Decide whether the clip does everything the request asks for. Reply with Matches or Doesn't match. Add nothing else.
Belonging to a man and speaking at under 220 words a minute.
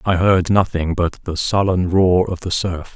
Matches